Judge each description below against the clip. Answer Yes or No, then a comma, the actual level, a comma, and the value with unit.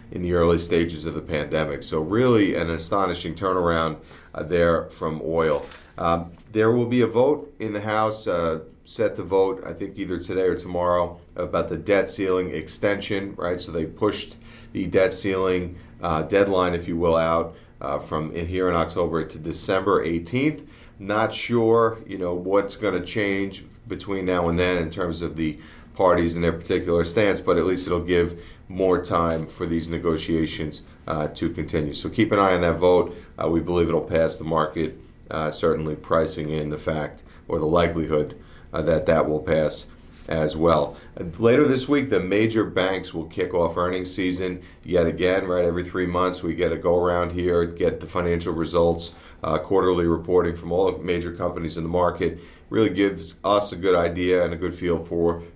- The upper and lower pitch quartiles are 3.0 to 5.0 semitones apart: No, narrow, 2.5 semitones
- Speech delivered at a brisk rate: No, average, 190 wpm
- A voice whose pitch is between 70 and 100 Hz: Yes, very low, 85 Hz